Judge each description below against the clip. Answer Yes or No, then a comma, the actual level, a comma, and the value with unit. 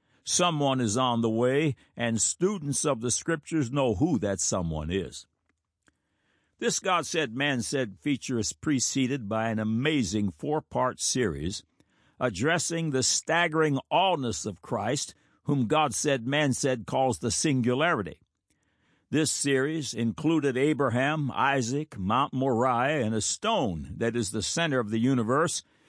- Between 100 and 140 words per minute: Yes, slow, 135 wpm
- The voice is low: Yes, low, 130 Hz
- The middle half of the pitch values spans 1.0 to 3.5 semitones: No, average, 4.0 semitones